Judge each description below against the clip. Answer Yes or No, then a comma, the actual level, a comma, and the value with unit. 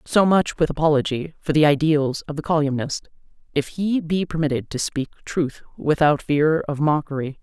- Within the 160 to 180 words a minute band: Yes, average, 170 wpm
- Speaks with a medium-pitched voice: Yes, medium, 150 Hz